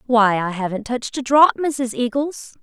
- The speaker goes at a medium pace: Yes, average, 185 wpm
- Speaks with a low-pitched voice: No, high, 245 Hz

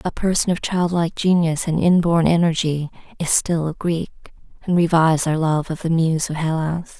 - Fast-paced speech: No, average, 180 wpm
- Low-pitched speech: No, medium, 165 Hz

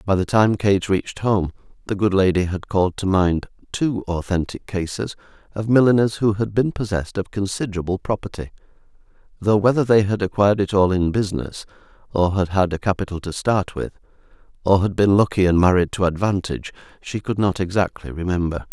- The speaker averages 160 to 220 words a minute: Yes, average, 175 wpm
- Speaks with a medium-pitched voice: No, low, 100 Hz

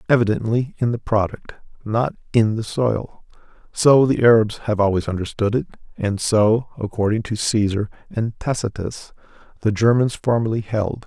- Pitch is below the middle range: Yes, low, 110 Hz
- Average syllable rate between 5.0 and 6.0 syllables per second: No, 4.8 syllables/s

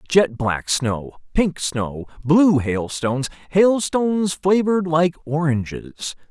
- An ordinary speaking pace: No, slow, 75 wpm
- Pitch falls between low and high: Yes, medium, 155 Hz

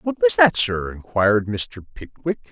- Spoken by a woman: No, male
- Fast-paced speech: No, average, 165 wpm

